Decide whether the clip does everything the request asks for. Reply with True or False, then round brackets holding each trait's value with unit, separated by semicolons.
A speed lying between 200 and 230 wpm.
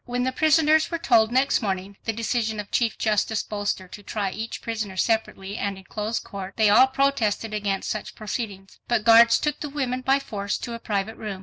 True (205 wpm)